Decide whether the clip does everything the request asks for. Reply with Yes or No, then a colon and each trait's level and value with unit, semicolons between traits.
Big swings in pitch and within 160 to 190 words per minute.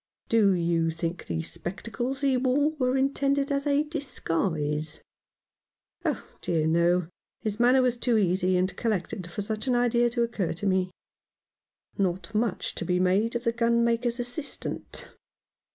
Yes: wide, 5.7 semitones; average, 165 wpm